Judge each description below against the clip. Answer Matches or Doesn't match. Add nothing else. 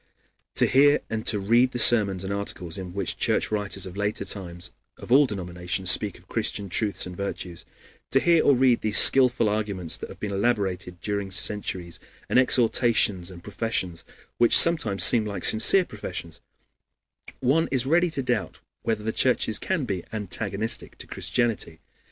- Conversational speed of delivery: Matches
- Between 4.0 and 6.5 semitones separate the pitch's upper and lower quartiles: Matches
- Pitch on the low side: Matches